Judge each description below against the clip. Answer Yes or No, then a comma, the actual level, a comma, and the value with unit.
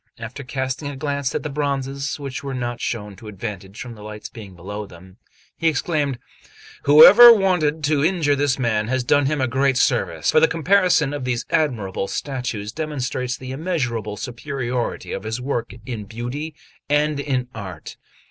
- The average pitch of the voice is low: Yes, low, 130 Hz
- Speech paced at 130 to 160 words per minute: No, average, 170 wpm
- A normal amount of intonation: Yes, average, 4.2 semitones